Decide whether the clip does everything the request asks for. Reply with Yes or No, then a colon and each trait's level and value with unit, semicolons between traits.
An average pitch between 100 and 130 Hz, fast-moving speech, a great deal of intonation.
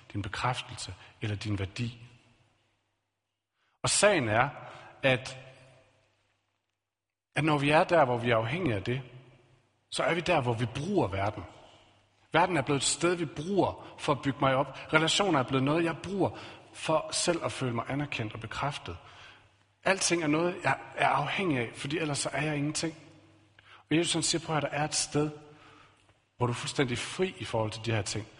No: low, 125 Hz; average, 190 wpm; wide, 5.9 semitones